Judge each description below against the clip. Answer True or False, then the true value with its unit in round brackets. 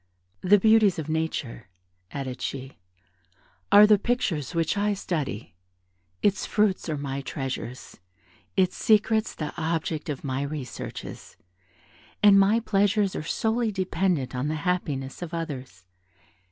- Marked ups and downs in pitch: True (6.6 semitones)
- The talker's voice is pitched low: False (165 Hz)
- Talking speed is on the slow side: True (125 wpm)